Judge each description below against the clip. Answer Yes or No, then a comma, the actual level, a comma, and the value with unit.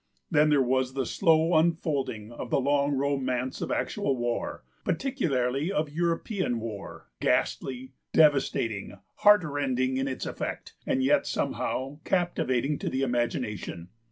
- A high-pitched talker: No, low, 135 Hz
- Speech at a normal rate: No, slow, 130 wpm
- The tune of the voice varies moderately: Yes, average, 3.5 semitones